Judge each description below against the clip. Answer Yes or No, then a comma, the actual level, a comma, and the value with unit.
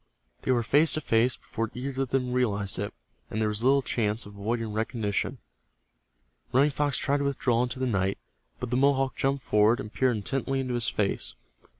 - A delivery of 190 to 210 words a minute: Yes, average, 195 wpm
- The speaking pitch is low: Yes, low, 125 Hz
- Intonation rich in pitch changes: No, average, 3.8 semitones